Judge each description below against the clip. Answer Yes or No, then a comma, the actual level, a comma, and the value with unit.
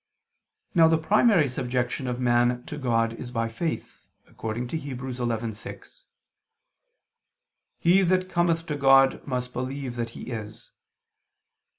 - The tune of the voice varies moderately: Yes, average, 4.8 semitones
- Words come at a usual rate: No, slow, 125 wpm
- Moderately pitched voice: No, low, 125 Hz